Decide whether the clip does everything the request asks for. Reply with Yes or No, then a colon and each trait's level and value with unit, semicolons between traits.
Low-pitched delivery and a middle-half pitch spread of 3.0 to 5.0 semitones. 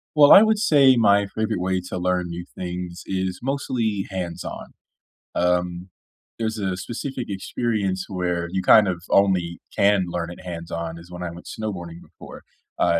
Yes: very low, 95 Hz; average, 3.6 semitones